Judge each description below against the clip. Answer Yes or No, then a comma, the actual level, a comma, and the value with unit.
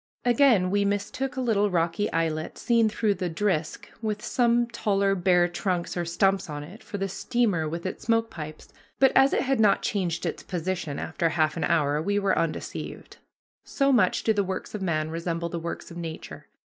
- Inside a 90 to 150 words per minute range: No, average, 195 wpm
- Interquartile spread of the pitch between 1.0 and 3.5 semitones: No, average, 4.3 semitones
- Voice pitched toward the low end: No, high, 190 Hz